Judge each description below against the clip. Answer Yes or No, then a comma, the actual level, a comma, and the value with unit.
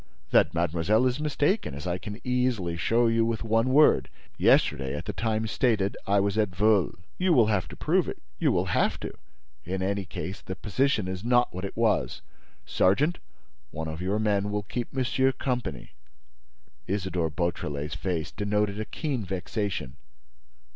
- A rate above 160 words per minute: Yes, average, 170 wpm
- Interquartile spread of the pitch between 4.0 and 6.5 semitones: Yes, average, 4.5 semitones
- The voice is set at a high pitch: No, low, 105 Hz